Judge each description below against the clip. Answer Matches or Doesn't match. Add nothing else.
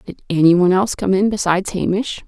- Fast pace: Matches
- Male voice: Doesn't match